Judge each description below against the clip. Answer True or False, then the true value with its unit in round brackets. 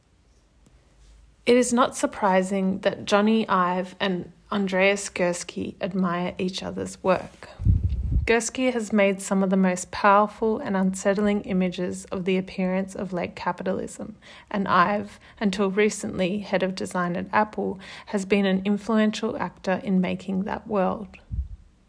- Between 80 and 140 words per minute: True (135 wpm)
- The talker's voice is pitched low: False (190 Hz)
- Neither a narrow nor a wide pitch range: False (2.3 semitones)